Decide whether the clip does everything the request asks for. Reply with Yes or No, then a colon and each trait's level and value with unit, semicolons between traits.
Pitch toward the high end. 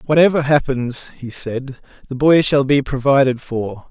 No: low, 135 Hz